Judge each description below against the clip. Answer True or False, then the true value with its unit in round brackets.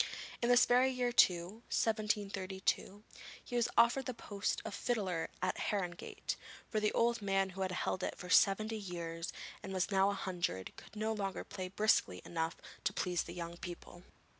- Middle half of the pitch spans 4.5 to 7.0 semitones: False (3.5 semitones)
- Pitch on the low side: False (195 Hz)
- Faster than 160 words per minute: True (175 wpm)